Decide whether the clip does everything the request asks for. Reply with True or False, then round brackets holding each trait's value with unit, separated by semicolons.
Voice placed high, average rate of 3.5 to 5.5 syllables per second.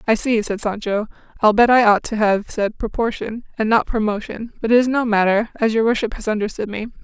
False (220 Hz; 5.7 syllables/s)